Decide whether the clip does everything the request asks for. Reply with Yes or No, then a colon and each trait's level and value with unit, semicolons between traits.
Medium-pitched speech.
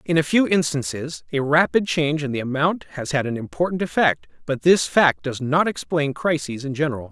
Yes: medium, 150 Hz